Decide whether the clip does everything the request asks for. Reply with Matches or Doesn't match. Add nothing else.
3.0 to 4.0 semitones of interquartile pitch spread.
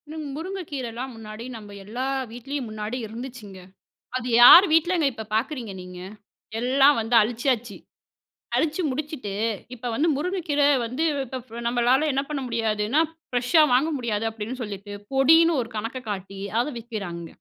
Doesn't match